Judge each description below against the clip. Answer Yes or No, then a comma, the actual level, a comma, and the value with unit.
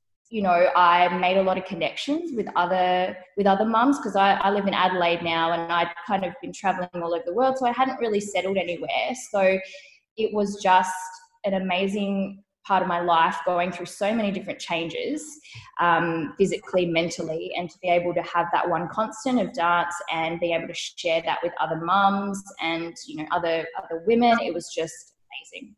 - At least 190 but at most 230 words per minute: Yes, average, 200 wpm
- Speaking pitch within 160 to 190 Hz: Yes, medium, 185 Hz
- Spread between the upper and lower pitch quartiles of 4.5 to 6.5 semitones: No, average, 2.7 semitones